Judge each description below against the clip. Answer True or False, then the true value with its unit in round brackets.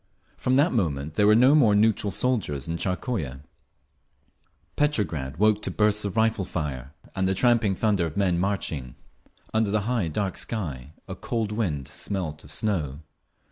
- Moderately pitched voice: False (100 Hz)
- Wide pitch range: True (6.0 semitones)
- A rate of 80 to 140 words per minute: False (160 wpm)